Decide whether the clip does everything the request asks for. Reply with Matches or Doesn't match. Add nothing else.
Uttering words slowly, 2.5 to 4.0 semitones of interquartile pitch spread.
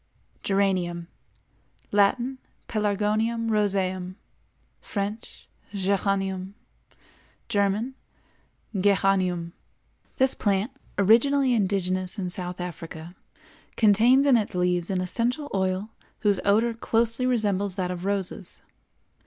Matches